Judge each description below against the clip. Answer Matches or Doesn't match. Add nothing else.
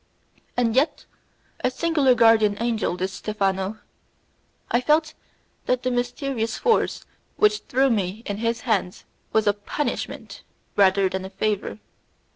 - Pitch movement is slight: Doesn't match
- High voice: Matches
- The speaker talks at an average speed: Doesn't match